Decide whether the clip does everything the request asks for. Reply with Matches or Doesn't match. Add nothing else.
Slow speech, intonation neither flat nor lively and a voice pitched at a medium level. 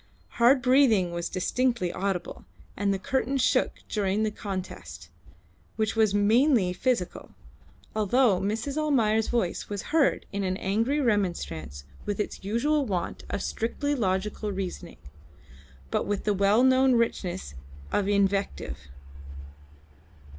Doesn't match